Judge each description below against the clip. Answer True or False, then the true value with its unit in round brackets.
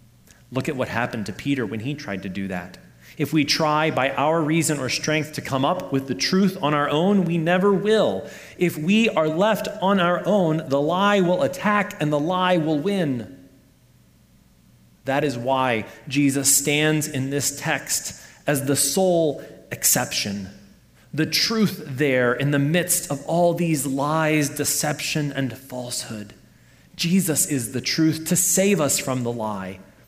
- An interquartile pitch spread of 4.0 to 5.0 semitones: True (4.7 semitones)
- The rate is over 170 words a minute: False (165 wpm)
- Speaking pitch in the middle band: True (145 Hz)